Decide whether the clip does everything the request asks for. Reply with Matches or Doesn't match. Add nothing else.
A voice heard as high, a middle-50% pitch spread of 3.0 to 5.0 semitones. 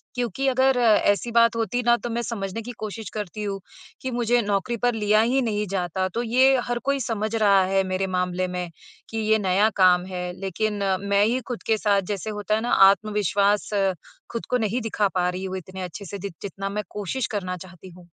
Matches